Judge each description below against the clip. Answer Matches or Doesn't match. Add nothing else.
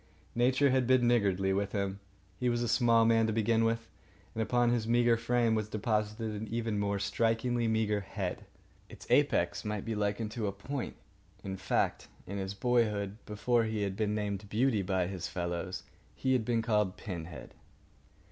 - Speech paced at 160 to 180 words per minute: Matches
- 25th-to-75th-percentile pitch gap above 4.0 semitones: Doesn't match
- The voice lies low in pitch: Matches